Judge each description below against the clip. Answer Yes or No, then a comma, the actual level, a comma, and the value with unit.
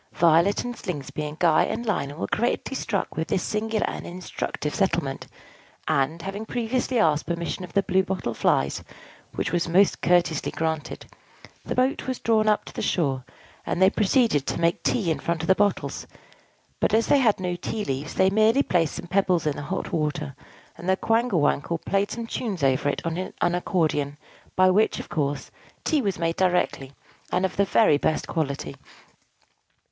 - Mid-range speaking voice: Yes, medium, 180 Hz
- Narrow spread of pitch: No, average, 4.9 semitones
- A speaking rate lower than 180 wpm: No, average, 185 wpm